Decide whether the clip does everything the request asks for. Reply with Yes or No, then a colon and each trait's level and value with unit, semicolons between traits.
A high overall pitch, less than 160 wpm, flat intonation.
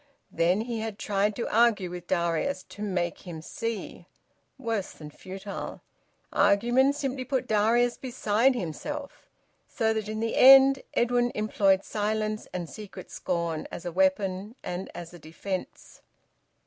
No: high, 210 Hz; average, 140 wpm; average, 4.5 semitones